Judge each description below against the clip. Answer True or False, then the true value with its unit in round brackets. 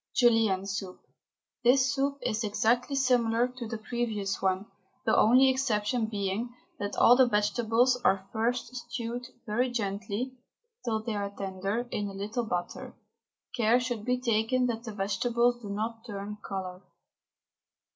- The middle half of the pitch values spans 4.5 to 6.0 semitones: False (3.2 semitones)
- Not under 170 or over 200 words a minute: False (145 wpm)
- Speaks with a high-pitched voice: True (225 Hz)